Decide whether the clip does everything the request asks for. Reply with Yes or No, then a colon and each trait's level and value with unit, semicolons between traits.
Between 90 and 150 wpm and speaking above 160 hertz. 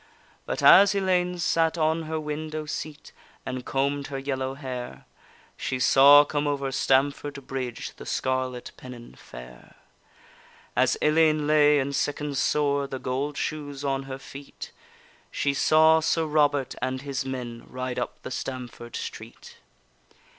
No: average, 140 wpm; medium, 140 Hz